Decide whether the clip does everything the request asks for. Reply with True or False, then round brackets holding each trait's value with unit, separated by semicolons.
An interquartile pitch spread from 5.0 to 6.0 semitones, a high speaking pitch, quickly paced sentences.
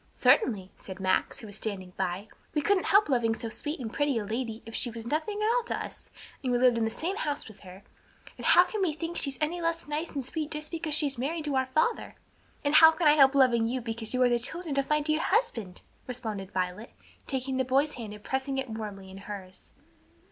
True (5.6 semitones; 260 Hz; 235 wpm)